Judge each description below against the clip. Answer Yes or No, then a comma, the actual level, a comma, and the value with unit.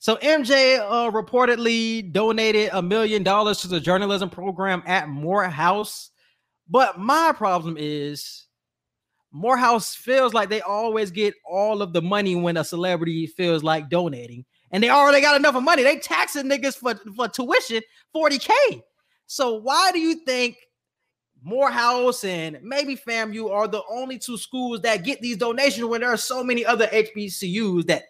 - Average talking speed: Yes, average, 160 wpm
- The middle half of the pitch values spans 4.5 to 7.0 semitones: Yes, average, 5.1 semitones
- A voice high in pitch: Yes, high, 220 Hz